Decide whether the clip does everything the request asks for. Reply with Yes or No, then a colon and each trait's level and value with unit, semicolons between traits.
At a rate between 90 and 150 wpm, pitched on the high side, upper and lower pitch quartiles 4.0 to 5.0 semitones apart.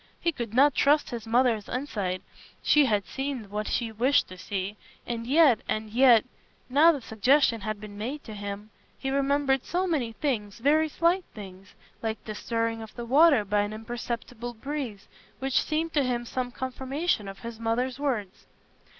No: average, 170 wpm; high, 240 Hz; average, 4.4 semitones